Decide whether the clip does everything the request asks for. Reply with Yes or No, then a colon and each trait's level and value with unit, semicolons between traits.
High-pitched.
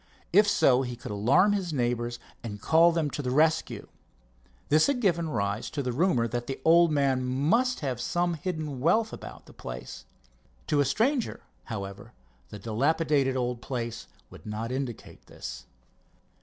No: low, 135 Hz